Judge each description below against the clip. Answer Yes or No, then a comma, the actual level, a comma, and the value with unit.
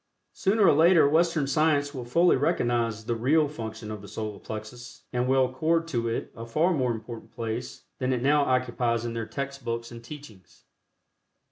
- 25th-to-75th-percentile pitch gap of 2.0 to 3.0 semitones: No, average, 4.2 semitones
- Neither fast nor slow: Yes, average, 180 wpm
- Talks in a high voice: No, low, 125 Hz